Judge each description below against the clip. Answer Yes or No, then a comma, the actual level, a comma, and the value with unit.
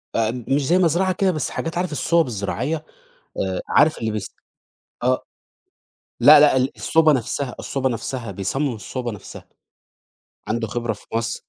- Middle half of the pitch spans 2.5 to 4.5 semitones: No, wide, 5.4 semitones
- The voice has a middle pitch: No, low, 130 Hz